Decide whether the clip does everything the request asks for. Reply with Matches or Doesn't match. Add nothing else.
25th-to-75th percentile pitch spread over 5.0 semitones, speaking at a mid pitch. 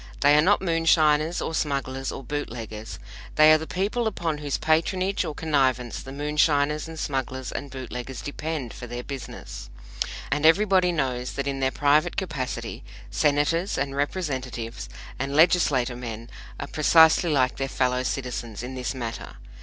Doesn't match